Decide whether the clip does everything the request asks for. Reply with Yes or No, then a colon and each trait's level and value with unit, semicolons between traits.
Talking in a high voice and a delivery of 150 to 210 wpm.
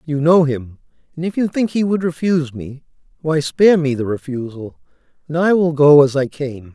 No: medium, 150 Hz; fast, 205 wpm